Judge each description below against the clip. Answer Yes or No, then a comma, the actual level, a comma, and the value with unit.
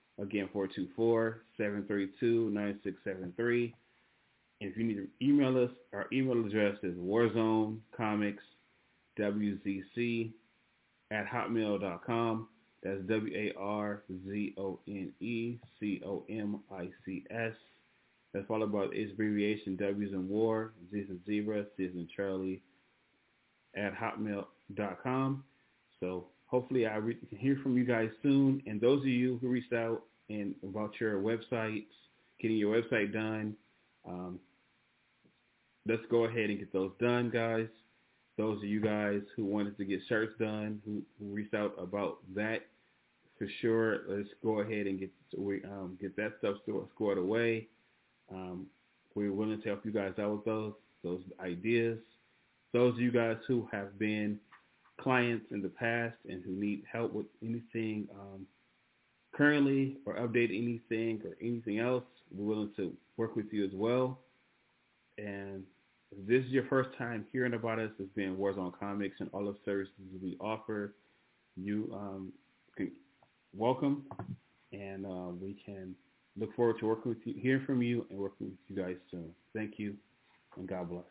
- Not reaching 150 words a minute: Yes, average, 140 wpm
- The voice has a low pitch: Yes, low, 105 Hz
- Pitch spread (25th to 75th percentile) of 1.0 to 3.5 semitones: Yes, average, 2.7 semitones